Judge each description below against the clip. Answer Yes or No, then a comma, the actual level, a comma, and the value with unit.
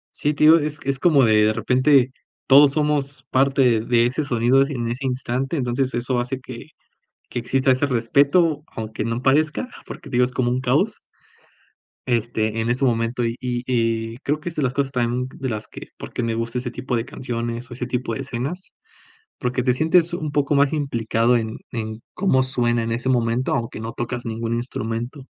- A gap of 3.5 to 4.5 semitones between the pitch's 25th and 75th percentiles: No, average, 2.8 semitones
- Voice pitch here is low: Yes, low, 125 Hz